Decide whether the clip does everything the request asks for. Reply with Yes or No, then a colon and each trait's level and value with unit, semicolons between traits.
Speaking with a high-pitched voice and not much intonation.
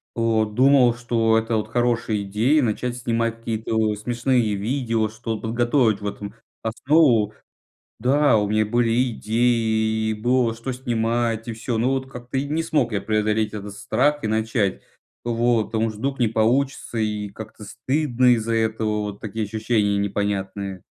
No: low, 115 Hz; narrow, 2.2 semitones